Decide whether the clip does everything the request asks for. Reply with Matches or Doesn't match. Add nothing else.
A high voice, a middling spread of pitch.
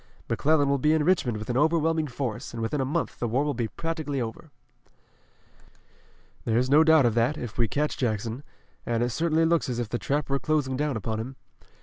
Doesn't match